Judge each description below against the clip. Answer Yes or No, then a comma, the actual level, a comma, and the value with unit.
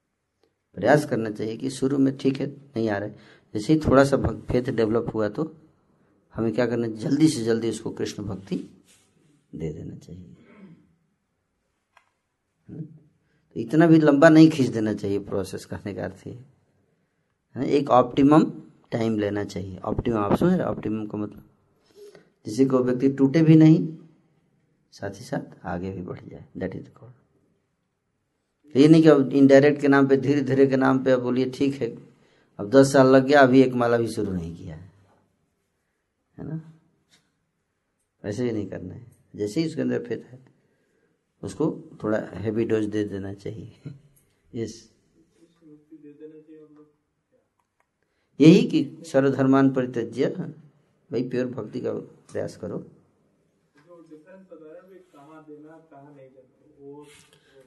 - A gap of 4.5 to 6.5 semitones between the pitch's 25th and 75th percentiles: Yes, average, 5.3 semitones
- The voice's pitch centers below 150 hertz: Yes, low, 135 Hz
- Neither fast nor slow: Yes, average, 140 wpm